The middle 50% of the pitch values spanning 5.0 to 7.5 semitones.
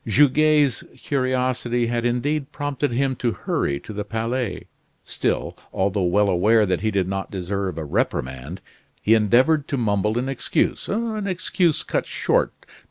Yes: wide, 5.5 semitones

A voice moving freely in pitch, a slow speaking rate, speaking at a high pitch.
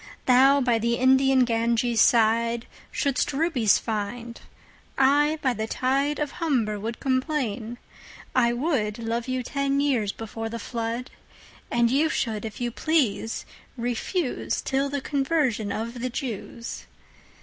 No: average, 3.2 semitones; slow, 115 wpm; high, 245 Hz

